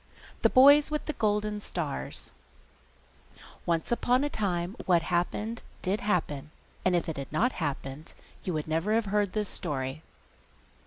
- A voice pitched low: No, medium, 185 Hz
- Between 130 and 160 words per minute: Yes, average, 150 wpm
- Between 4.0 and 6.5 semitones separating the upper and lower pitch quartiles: Yes, average, 5.3 semitones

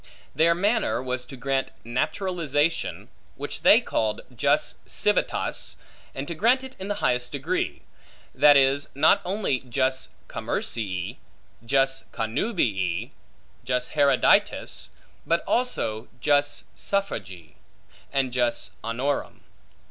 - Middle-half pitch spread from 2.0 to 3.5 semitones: No, average, 5.3 semitones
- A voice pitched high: No, low, 135 Hz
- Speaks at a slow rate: Yes, slow, 110 wpm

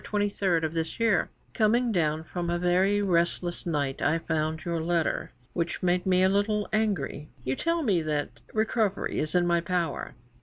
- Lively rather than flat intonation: No, average, 4.0 semitones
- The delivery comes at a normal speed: Yes, average, 175 wpm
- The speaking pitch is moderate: Yes, medium, 175 Hz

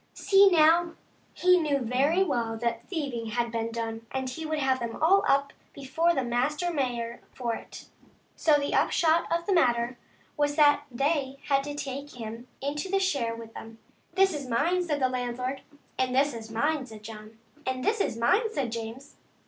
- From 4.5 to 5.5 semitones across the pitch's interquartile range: Yes, average, 5.0 semitones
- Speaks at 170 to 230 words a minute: Yes, average, 195 wpm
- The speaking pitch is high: Yes, very high, 275 Hz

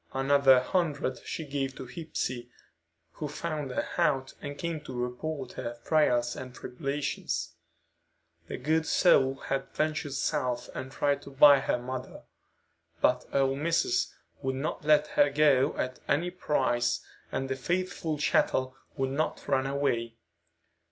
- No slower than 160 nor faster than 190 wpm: No, average, 140 wpm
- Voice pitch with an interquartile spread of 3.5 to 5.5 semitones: No, average, 2.8 semitones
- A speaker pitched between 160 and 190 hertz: No, low, 135 Hz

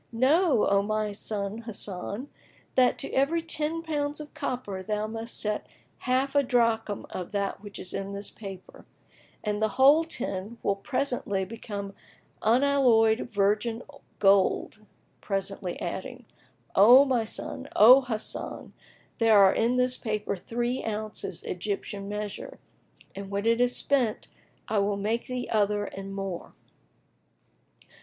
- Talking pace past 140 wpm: No, slow, 135 wpm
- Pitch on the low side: No, high, 220 Hz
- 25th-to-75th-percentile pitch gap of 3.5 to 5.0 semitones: Yes, average, 3.9 semitones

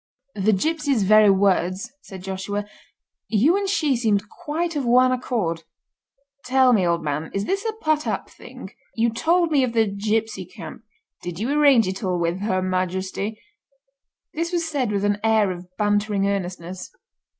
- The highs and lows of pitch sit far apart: Yes, wide, 5.8 semitones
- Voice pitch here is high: Yes, high, 215 Hz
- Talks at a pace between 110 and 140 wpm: No, average, 160 wpm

